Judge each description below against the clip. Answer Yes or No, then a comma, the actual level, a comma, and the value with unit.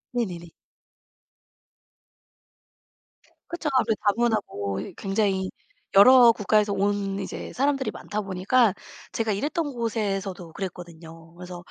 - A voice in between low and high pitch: No, high, 200 Hz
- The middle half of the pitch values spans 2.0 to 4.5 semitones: Yes, average, 4.1 semitones